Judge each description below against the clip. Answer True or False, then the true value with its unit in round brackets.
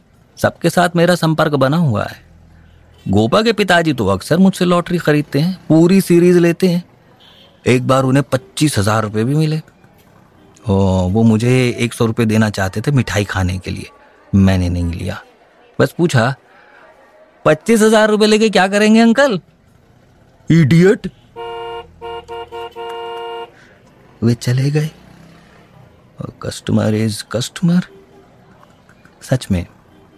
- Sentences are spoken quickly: False (125 wpm)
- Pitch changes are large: True (7.7 semitones)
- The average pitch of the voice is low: True (125 Hz)